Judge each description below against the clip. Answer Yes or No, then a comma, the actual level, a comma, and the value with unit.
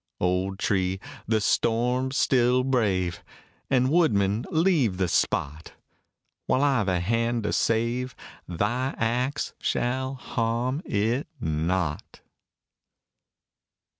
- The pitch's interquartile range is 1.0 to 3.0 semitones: No, average, 5.0 semitones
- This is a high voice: No, low, 115 Hz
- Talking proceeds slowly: Yes, slow, 100 wpm